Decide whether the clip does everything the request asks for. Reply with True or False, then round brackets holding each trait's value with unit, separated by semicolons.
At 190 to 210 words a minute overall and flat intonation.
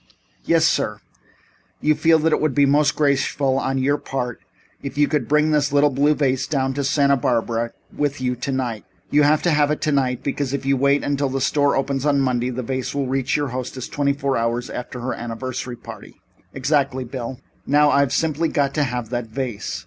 True (200 wpm; 2.3 semitones)